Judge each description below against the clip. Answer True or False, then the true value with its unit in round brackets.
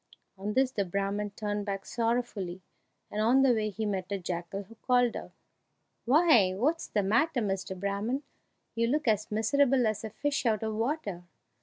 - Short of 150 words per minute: False (175 wpm)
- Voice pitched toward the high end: True (215 Hz)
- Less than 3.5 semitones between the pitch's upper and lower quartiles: False (3.8 semitones)